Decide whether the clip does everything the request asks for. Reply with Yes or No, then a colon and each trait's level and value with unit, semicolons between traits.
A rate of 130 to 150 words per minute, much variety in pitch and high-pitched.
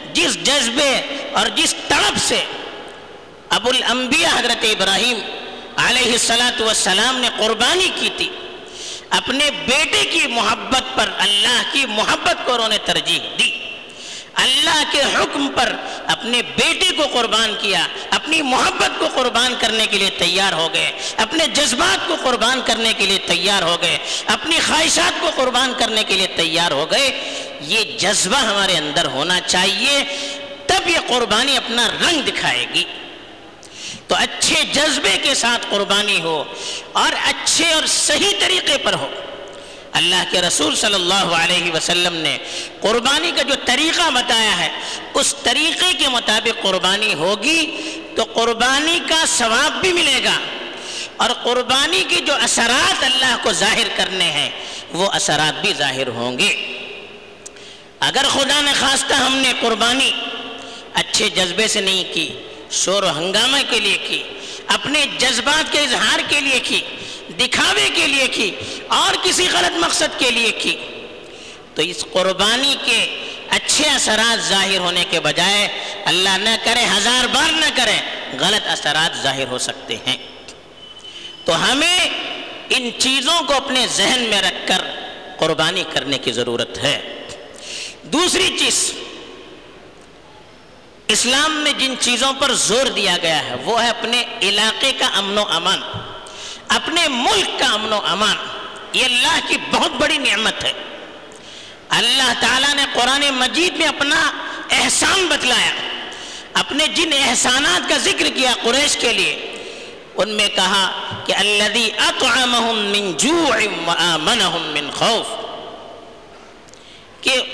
Yes: average, 140 wpm; wide, 6.5 semitones; high, 240 Hz